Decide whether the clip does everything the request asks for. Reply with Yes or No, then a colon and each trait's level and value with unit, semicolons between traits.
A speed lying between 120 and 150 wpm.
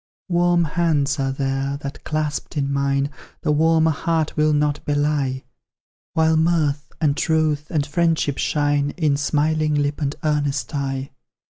Yes: average, 140 wpm